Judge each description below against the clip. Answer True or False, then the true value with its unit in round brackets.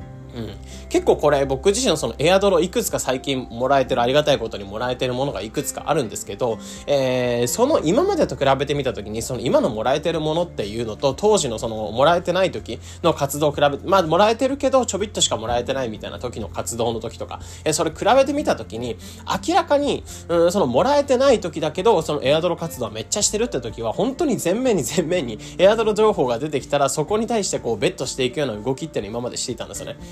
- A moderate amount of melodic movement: False (8.3 semitones)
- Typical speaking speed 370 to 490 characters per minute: True (480 characters per minute)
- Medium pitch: True (145 Hz)